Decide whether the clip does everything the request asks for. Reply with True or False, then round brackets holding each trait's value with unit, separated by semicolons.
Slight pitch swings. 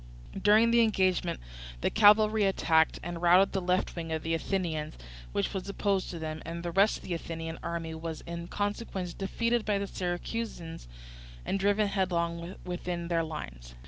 False (3.2 semitones)